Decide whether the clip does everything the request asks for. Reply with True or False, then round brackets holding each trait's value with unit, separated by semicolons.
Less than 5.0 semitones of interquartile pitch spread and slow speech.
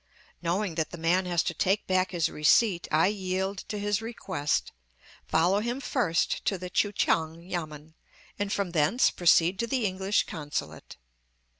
False (3.6 semitones; 160 wpm)